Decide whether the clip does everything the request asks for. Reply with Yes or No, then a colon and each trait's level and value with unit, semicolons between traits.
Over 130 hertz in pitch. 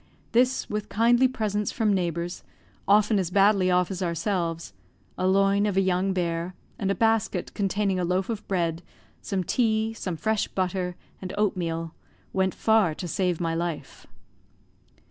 Yes: high, 190 Hz